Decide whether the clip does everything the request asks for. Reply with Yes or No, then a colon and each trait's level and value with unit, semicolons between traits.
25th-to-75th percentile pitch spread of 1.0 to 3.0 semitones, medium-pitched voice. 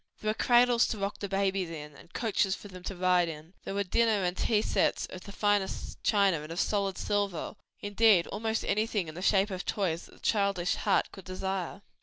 No: narrow, 2.4 semitones; high, 195 Hz